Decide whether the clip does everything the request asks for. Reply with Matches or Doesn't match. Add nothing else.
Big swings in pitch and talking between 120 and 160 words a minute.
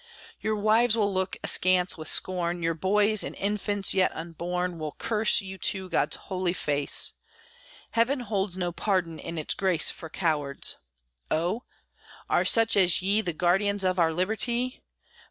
Doesn't match